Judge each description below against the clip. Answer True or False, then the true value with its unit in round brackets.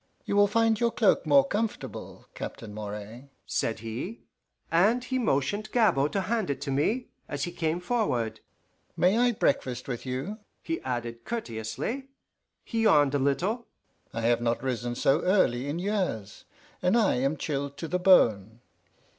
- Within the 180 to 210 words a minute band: False (160 wpm)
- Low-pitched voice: False (145 Hz)